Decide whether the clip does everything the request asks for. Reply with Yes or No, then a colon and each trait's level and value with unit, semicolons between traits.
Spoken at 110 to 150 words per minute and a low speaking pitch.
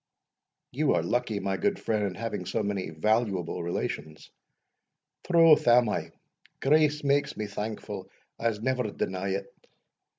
Yes: slow, 135 wpm; low, 110 Hz